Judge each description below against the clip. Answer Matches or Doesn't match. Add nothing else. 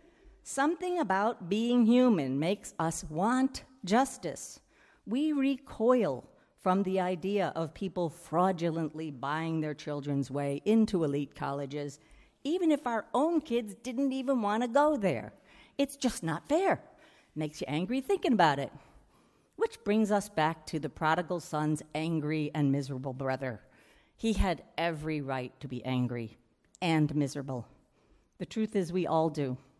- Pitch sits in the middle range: Matches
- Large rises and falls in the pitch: Matches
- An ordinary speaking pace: Matches